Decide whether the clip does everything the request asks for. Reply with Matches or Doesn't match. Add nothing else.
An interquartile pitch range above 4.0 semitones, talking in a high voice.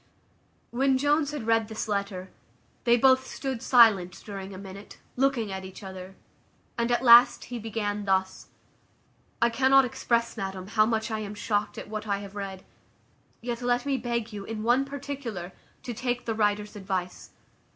Doesn't match